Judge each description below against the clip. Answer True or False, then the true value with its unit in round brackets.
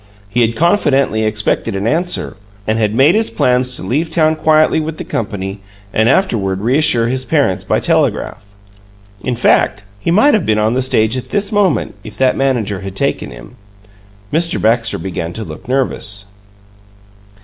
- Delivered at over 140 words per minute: True (170 wpm)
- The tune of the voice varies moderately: False (6.6 semitones)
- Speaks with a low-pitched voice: True (125 Hz)